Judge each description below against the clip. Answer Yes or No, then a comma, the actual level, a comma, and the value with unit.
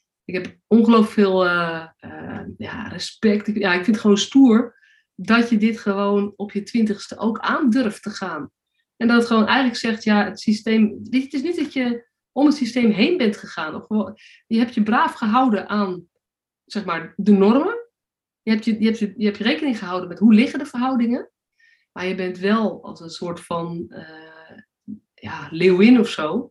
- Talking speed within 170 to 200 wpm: Yes, average, 190 wpm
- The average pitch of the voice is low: No, high, 220 Hz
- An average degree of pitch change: Yes, average, 3.3 semitones